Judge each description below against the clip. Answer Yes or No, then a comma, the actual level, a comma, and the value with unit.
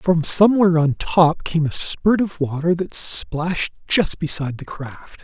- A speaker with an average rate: Yes, average, 170 wpm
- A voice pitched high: No, medium, 165 Hz